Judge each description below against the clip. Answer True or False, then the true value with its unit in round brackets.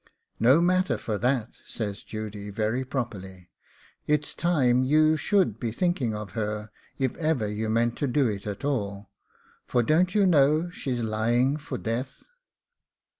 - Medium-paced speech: True (150 wpm)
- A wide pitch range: True (5.7 semitones)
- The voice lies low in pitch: True (120 Hz)